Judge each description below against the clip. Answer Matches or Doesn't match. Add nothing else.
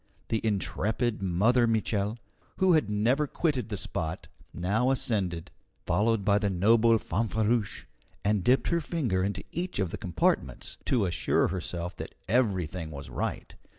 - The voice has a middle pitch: Doesn't match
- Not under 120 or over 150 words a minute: Matches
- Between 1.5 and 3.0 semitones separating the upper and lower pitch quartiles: Doesn't match